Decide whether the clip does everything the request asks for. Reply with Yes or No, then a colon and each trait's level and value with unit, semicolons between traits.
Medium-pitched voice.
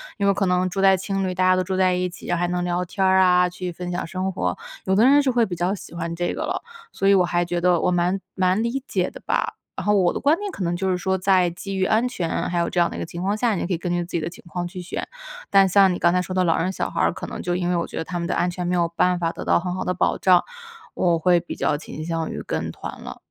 Yes: medium, 180 Hz